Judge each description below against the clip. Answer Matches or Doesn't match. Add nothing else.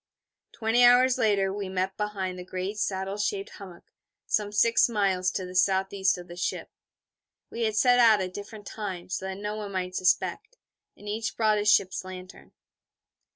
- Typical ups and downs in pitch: Doesn't match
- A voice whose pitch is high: Matches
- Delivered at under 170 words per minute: Doesn't match